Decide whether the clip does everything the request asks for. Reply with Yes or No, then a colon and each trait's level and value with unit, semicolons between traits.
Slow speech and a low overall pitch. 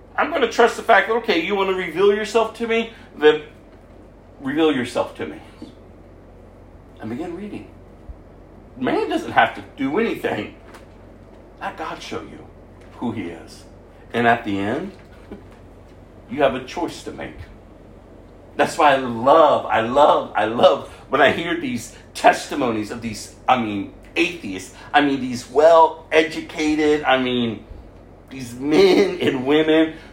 No: average, 145 wpm; low, 120 Hz